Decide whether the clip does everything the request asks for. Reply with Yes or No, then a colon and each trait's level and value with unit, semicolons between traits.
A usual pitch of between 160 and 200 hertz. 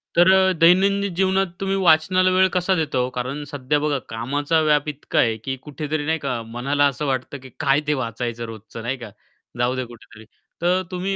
No: medium, 145 Hz